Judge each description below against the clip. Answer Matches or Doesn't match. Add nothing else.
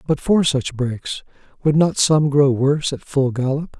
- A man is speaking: Matches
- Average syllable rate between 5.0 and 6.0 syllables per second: Doesn't match